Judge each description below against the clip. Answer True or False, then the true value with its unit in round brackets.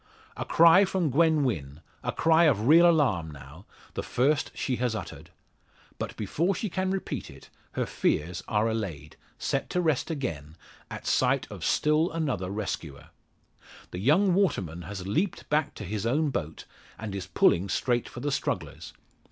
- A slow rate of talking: False (165 wpm)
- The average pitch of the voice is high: False (125 Hz)